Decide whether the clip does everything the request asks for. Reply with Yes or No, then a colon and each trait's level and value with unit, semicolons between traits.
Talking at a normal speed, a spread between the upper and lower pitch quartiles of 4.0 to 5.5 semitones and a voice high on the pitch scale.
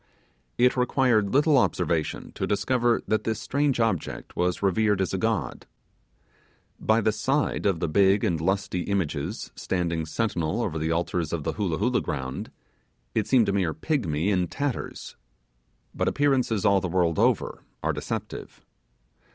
No: average, 150 wpm; average, 5.2 semitones; low, 100 Hz